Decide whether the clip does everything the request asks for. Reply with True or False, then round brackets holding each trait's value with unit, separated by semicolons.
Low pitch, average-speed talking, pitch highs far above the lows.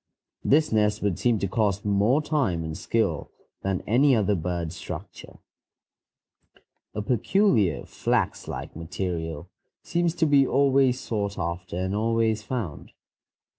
False (105 Hz; 130 wpm; 6.0 semitones)